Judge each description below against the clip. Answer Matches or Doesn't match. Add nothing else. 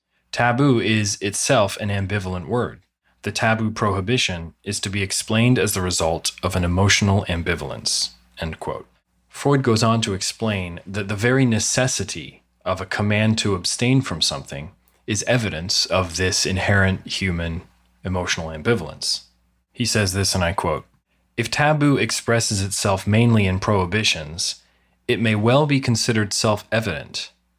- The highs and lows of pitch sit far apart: Doesn't match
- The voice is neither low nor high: Doesn't match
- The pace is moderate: Matches